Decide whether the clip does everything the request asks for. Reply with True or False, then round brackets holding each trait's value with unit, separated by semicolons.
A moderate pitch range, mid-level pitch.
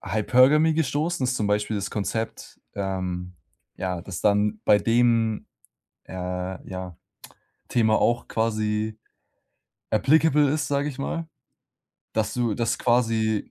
False (3.8 semitones; 110 Hz)